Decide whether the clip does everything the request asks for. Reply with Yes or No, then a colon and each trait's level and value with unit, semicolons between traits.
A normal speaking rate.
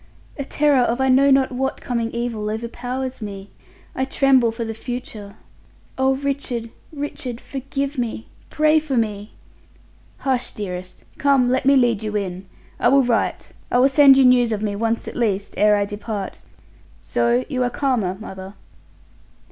Yes: average, 165 wpm